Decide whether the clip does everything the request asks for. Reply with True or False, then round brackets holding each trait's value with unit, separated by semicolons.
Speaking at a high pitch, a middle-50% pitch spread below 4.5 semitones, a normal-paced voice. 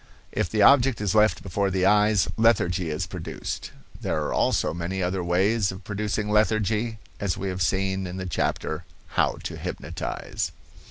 False (95 Hz; 2.8 semitones; 165 wpm)